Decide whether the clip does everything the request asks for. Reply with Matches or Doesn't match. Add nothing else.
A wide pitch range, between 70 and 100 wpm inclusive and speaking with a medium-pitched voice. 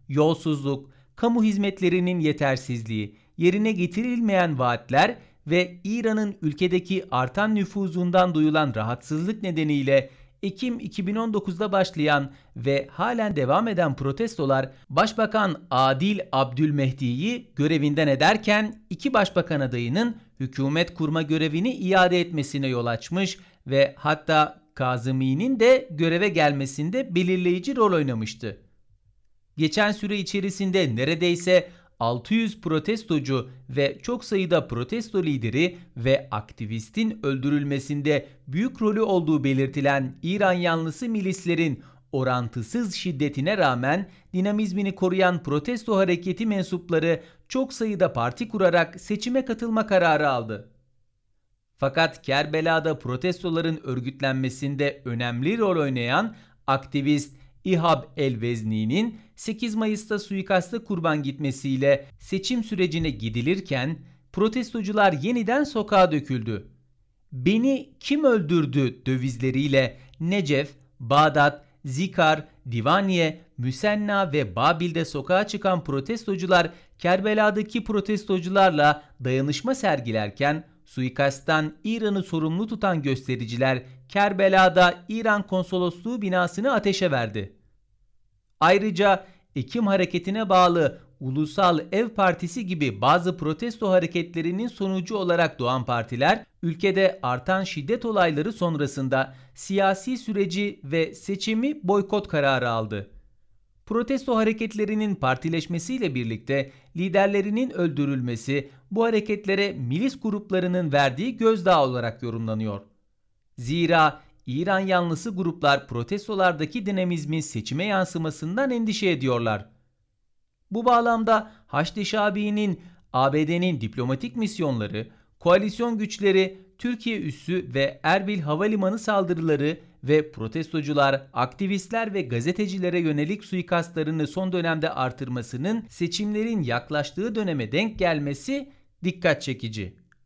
Matches